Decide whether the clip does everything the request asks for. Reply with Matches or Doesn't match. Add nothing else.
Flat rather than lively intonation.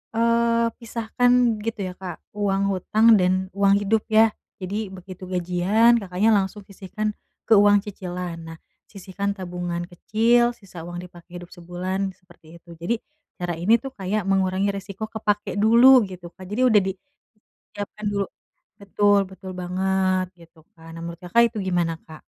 Doesn't match